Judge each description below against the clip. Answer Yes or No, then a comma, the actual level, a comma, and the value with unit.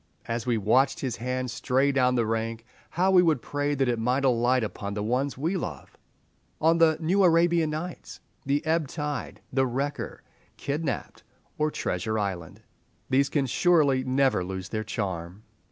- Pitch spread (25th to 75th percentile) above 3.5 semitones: Yes, average, 5.0 semitones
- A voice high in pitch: No, low, 130 Hz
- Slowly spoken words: No, average, 165 wpm